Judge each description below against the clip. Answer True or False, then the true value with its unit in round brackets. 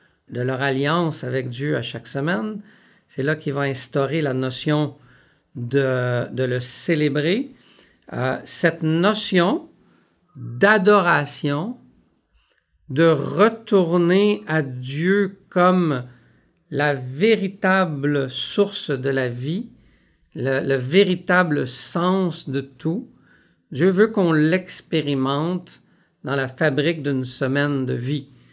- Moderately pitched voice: True (150 Hz)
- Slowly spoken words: True (105 wpm)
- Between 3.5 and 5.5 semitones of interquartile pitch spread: True (5.2 semitones)